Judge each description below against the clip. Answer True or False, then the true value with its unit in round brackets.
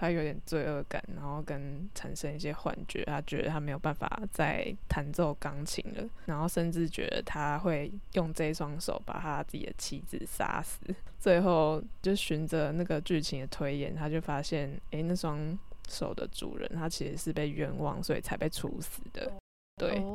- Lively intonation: False (2.7 semitones)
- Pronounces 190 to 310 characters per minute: True (260 characters per minute)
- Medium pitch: True (160 Hz)